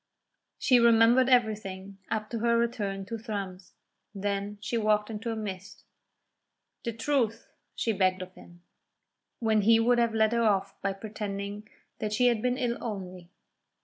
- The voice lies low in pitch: No, high, 215 Hz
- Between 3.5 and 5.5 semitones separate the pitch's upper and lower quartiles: No, average, 2.8 semitones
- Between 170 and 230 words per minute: No, average, 155 wpm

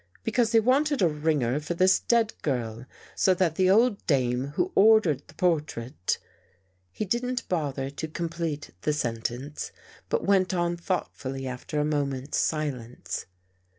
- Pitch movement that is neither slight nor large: No, wide, 5.9 semitones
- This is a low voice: No, medium, 155 Hz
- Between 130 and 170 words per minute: Yes, average, 150 wpm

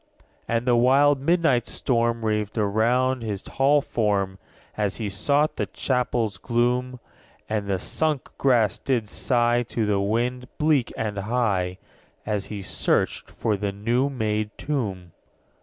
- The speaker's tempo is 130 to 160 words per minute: Yes, average, 145 wpm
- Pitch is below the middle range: Yes, low, 115 Hz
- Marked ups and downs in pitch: No, average, 3.5 semitones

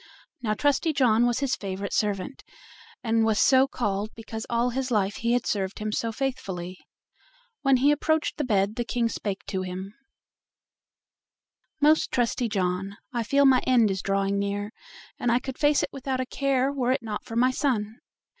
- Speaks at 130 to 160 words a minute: No, average, 180 wpm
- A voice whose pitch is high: Yes, high, 230 Hz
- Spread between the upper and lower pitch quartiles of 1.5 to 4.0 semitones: No, average, 4.4 semitones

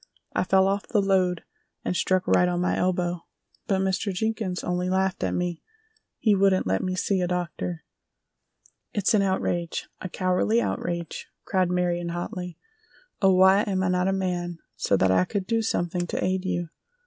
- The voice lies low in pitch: No, medium, 185 Hz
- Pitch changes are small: Yes, narrow, 1.6 semitones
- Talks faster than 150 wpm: Yes, average, 170 wpm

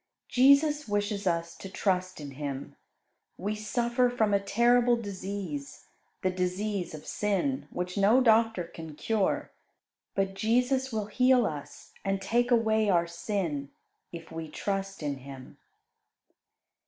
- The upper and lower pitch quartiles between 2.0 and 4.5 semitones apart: No, average, 5.1 semitones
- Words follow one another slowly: Yes, slow, 130 wpm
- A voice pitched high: Yes, high, 200 Hz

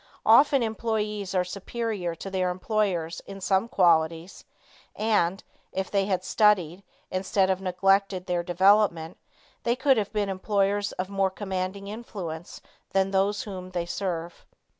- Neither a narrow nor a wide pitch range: No, narrow, 2.3 semitones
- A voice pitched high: Yes, high, 195 Hz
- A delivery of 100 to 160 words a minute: Yes, average, 140 wpm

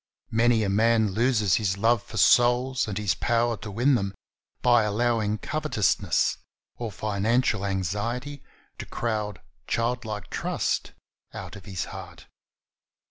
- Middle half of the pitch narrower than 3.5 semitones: Yes, average, 2.7 semitones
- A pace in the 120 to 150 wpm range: Yes, slow, 135 wpm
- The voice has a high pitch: No, low, 110 Hz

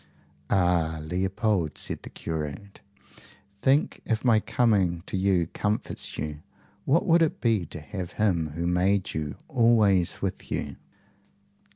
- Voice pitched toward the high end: No, very low, 95 Hz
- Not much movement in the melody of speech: No, average, 4.4 semitones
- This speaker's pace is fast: No, slow, 135 wpm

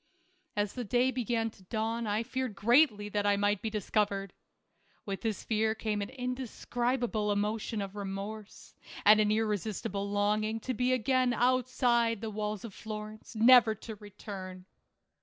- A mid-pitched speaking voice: No, high, 215 Hz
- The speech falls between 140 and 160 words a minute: Yes, average, 150 wpm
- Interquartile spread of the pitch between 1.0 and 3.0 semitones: Yes, narrow, 2.6 semitones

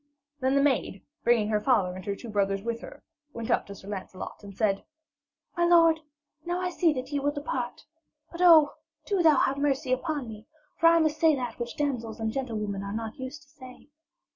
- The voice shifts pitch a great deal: Yes, wide, 5.8 semitones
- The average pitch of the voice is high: Yes, very high, 255 Hz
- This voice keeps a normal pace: No, fast, 210 wpm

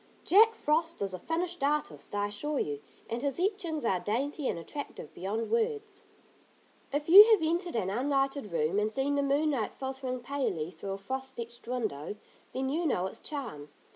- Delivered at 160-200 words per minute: Yes, average, 175 wpm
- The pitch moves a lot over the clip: Yes, wide, 7.1 semitones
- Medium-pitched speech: No, very high, 270 Hz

